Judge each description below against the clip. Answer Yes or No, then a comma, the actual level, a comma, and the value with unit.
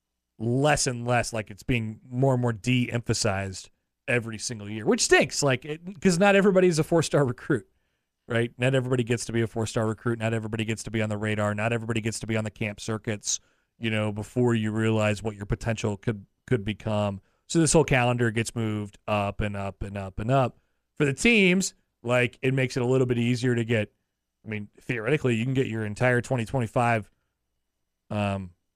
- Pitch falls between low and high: No, low, 115 Hz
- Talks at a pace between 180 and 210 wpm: Yes, fast, 205 wpm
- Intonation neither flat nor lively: Yes, average, 3.2 semitones